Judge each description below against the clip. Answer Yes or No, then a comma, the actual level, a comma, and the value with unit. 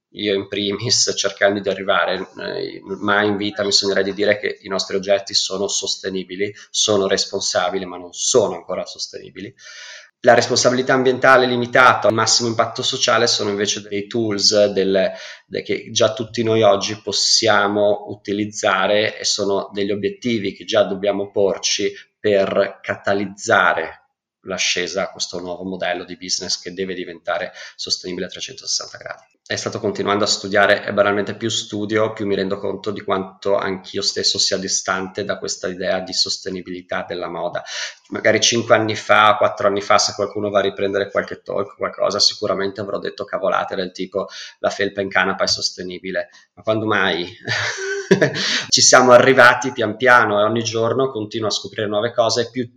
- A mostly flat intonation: Yes, narrow, 1.9 semitones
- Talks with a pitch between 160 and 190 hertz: No, low, 100 Hz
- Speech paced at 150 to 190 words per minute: Yes, average, 165 wpm